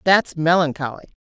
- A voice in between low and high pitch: Yes, medium, 160 Hz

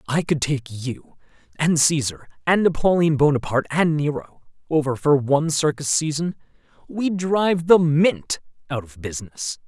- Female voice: No, male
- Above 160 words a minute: No, average, 150 wpm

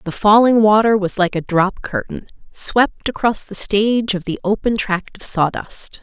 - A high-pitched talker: Yes, high, 210 Hz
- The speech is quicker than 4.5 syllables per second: No, 4.4 syllables/s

